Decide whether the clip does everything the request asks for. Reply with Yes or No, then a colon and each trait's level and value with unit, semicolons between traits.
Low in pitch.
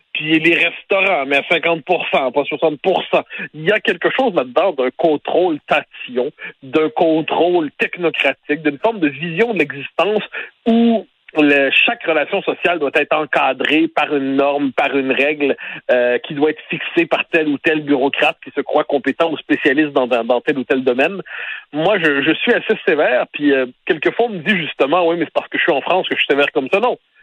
No: medium, 155 Hz